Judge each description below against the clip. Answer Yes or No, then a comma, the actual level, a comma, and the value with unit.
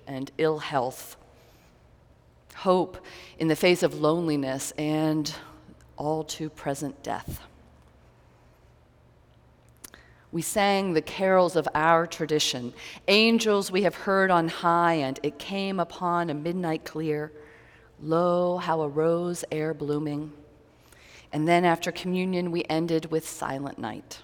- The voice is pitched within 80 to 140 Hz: No, medium, 160 Hz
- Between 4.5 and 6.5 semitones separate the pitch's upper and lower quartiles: No, average, 2.8 semitones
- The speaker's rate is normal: No, slow, 120 wpm